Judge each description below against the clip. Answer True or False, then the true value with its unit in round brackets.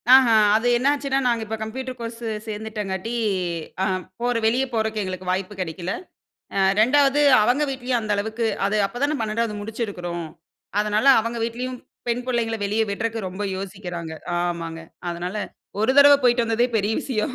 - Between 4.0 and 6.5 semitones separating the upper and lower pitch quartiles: False (3.6 semitones)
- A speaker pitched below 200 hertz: False (220 Hz)